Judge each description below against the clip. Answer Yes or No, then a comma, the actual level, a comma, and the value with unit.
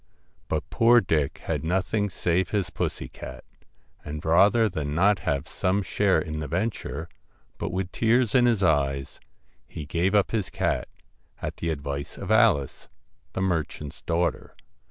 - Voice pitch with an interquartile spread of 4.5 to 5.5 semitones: Yes, average, 5.0 semitones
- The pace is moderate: Yes, average, 155 wpm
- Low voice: Yes, very low, 90 Hz